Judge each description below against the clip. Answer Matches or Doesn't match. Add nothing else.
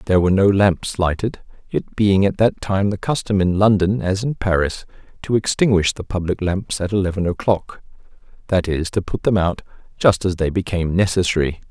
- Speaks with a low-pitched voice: Matches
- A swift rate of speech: Doesn't match